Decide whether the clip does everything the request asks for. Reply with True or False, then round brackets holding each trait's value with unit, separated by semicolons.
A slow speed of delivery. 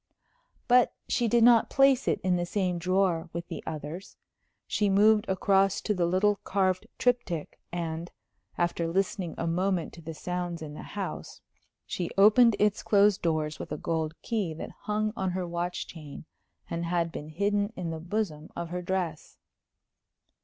False (165 wpm)